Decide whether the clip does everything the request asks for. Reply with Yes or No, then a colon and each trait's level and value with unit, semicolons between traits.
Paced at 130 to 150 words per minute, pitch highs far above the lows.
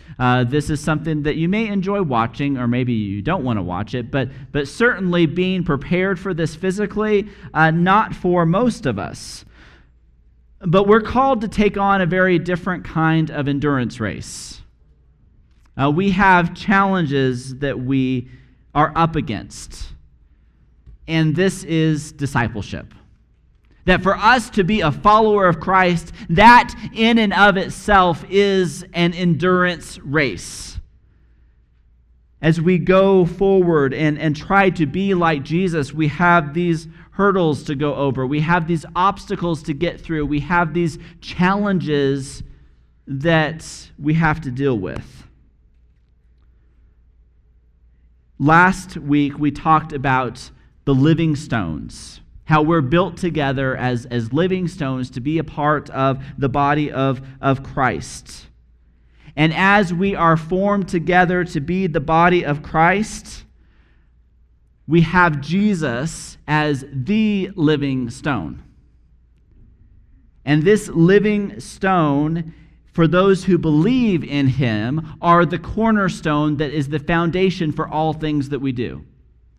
Yes: slow, 135 wpm; wide, 6.1 semitones